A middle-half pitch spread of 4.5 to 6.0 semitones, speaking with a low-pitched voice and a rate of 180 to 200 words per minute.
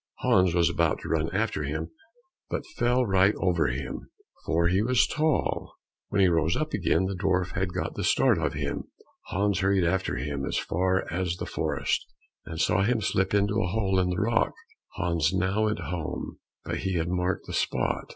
No: average, 2.9 semitones; very low, 95 Hz; average, 195 wpm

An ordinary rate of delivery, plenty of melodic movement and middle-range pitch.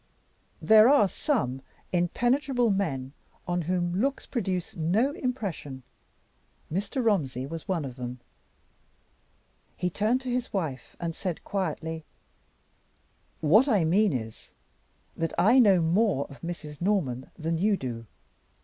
No: slow, 125 wpm; wide, 5.8 semitones; medium, 180 Hz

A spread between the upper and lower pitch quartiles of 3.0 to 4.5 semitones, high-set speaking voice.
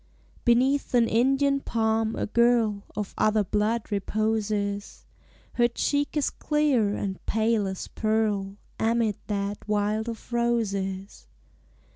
No: narrow, 2.5 semitones; high, 220 Hz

